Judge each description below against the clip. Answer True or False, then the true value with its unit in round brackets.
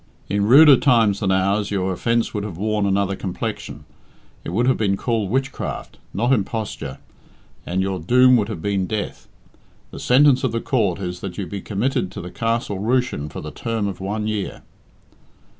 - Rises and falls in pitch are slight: False (3.5 semitones)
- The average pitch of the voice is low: True (105 Hz)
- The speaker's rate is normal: True (180 wpm)